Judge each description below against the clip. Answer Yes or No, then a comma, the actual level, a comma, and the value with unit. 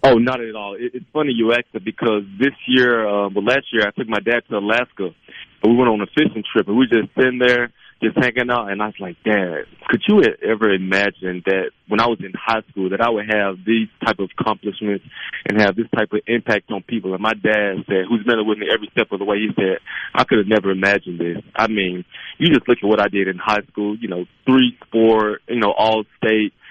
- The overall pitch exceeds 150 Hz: No, low, 110 Hz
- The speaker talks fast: Yes, fast, 250 wpm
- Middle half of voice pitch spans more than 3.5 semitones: No, average, 2.8 semitones